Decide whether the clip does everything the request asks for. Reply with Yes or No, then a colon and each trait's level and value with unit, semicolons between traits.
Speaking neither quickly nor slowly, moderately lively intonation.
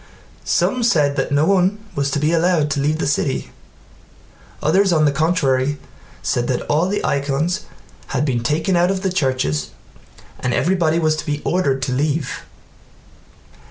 Yes: average, 160 wpm; average, 4.1 semitones